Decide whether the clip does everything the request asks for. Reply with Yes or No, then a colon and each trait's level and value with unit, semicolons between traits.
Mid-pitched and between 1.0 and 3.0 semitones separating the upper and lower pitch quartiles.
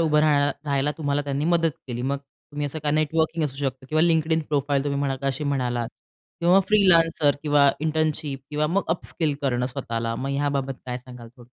Yes: medium, 145 Hz; narrow, 2.6 semitones